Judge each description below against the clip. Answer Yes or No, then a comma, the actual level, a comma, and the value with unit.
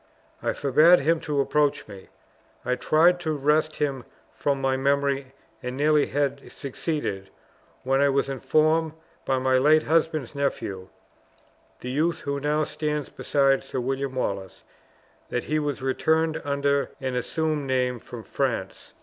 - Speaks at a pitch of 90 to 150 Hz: Yes, medium, 140 Hz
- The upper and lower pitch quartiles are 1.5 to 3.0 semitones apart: Yes, average, 2.7 semitones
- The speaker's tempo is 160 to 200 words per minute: No, average, 145 wpm